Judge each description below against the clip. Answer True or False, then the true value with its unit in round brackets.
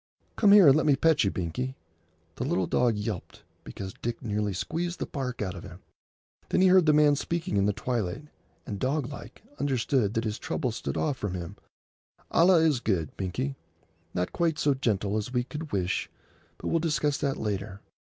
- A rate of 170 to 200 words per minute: True (185 wpm)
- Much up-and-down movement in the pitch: True (6.7 semitones)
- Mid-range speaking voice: False (125 Hz)